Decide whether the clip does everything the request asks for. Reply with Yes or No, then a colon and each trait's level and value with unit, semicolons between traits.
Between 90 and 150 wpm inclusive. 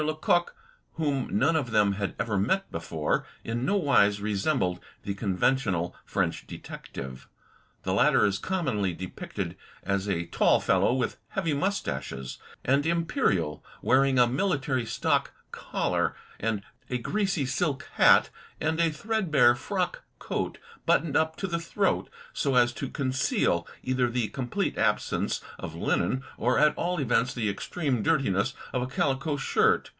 Yes: average, 145 wpm